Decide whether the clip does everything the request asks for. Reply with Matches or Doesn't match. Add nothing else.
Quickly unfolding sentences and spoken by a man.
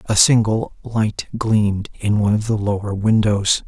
Doesn't match